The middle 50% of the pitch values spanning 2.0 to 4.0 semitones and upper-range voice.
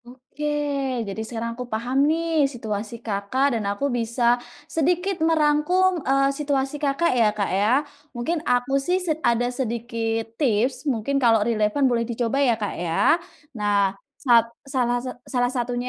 Yes: average, 3.6 semitones; high, 245 Hz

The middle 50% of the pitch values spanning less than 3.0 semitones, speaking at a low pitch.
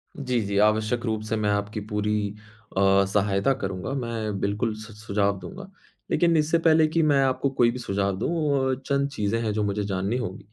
No: average, 4.4 semitones; low, 110 Hz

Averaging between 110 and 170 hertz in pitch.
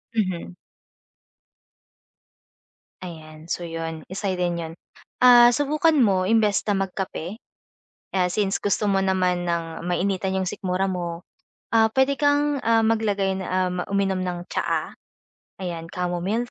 No: high, 190 Hz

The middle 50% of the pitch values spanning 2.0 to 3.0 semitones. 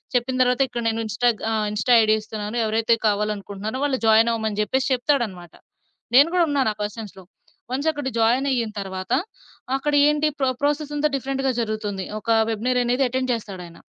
No: average, 3.8 semitones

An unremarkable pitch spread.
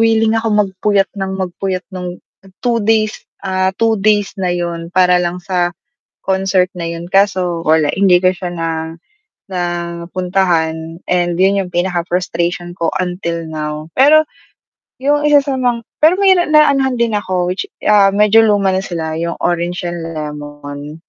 Yes: average, 3.3 semitones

